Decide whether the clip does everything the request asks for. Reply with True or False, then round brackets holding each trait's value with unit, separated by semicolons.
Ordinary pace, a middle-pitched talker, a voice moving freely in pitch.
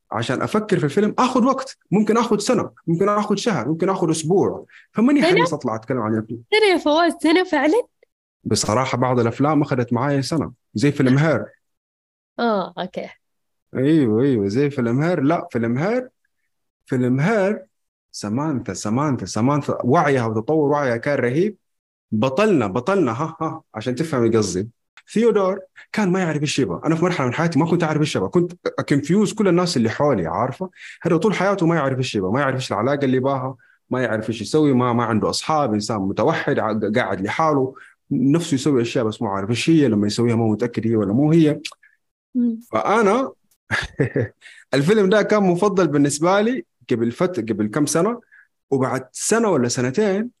False (165 wpm; 150 Hz; 7.9 semitones)